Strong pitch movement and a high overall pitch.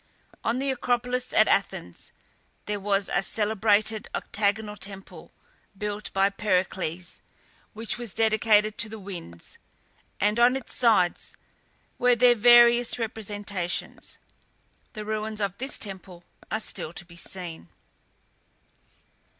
No: average, 2.8 semitones; high, 210 Hz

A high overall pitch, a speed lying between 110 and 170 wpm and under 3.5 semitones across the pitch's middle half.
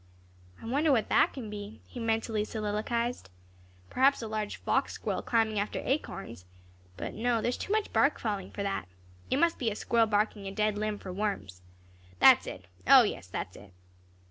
No: high, 215 Hz; average, 185 wpm; average, 2.9 semitones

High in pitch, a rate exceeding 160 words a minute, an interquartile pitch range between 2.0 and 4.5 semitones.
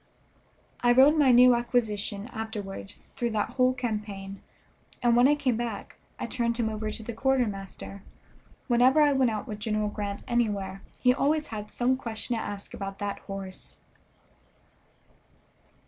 No: high, 225 Hz; average, 150 wpm; average, 3.4 semitones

